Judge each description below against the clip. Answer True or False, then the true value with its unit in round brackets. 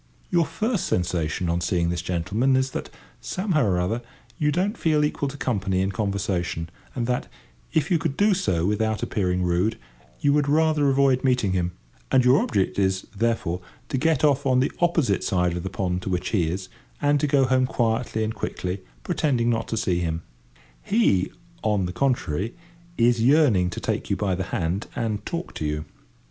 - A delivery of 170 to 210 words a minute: True (190 wpm)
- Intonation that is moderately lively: False (7.3 semitones)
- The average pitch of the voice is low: True (110 Hz)